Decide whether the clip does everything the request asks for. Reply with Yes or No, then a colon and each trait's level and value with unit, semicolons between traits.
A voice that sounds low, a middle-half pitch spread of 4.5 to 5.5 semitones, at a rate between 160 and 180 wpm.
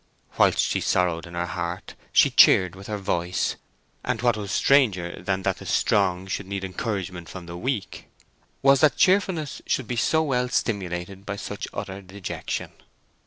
Yes: very low, 95 Hz; average, 5.2 semitones; average, 165 wpm